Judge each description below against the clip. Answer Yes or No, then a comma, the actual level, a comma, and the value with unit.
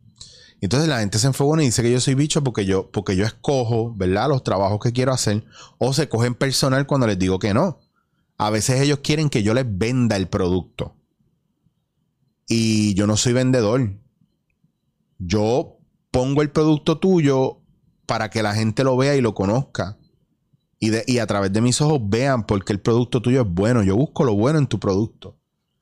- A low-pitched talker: Yes, low, 120 Hz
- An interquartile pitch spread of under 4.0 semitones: No, average, 4.3 semitones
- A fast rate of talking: Yes, fast, 195 wpm